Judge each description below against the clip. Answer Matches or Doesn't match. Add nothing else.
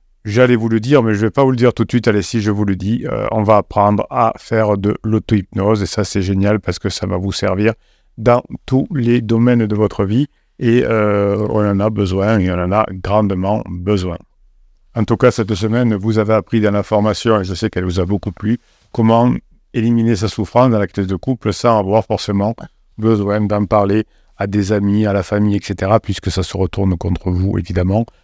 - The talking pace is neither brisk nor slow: Doesn't match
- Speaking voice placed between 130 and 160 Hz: Doesn't match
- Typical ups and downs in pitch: Doesn't match